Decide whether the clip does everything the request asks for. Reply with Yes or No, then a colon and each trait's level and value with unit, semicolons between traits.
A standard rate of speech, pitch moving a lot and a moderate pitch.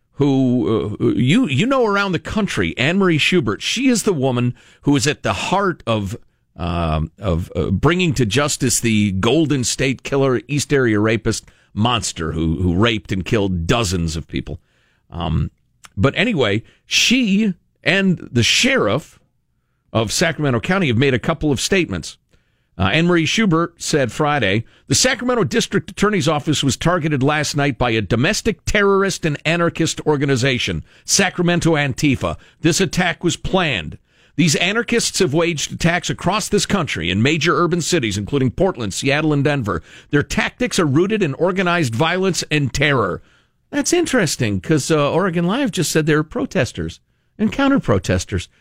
Yes: average, 155 wpm; wide, 7.4 semitones; medium, 150 Hz